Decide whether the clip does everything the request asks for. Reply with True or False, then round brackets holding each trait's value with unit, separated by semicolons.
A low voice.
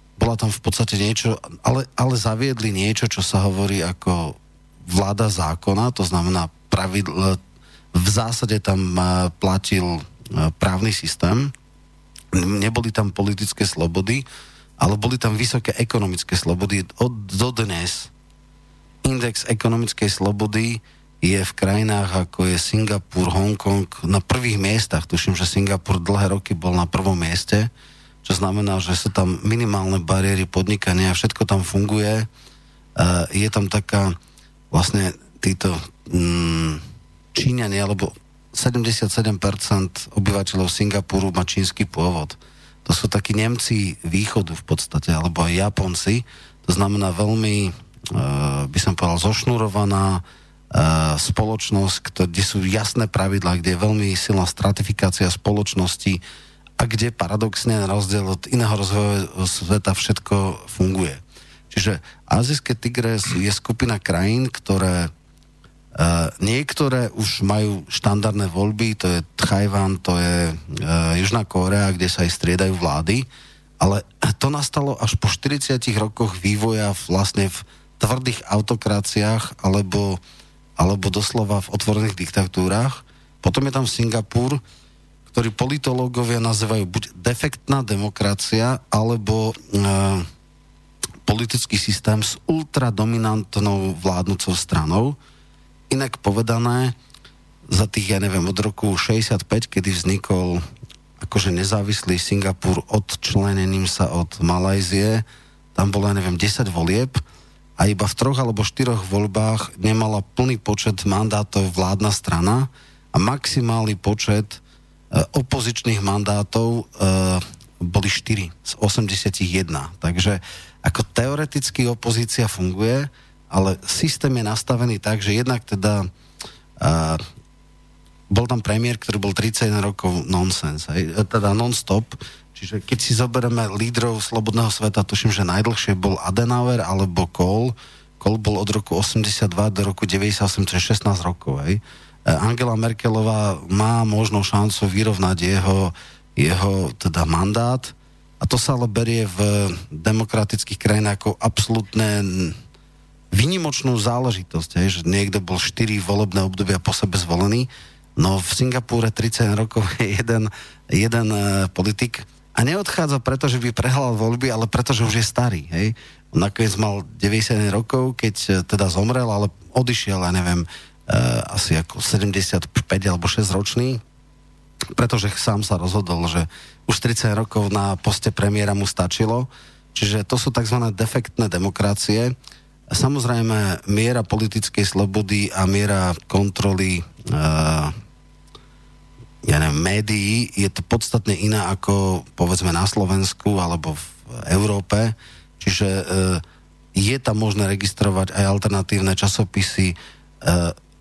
True (100 Hz)